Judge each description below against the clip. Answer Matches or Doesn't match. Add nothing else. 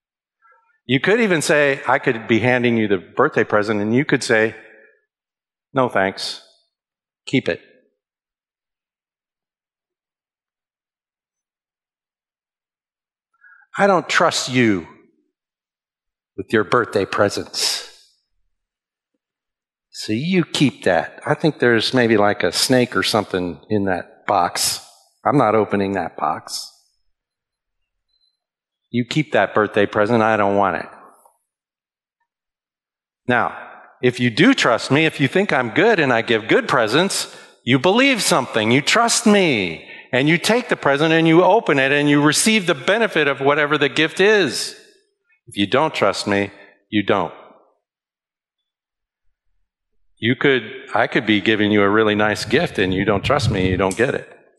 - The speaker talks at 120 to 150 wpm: Matches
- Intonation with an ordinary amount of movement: Doesn't match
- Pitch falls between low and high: Doesn't match